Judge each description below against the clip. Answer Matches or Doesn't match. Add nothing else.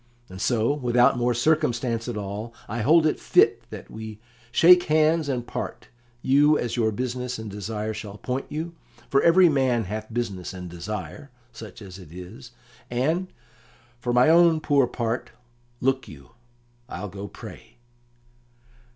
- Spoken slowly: Doesn't match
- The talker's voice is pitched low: Matches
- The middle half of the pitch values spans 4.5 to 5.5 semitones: Matches